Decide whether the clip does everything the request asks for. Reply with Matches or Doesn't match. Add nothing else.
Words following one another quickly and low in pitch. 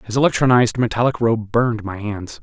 Doesn't match